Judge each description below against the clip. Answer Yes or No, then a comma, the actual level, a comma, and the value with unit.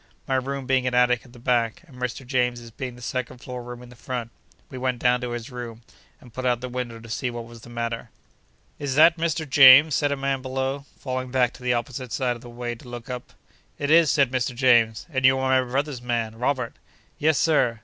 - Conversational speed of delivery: No, fast, 235 wpm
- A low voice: Yes, low, 125 Hz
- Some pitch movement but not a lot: No, narrow, 1.7 semitones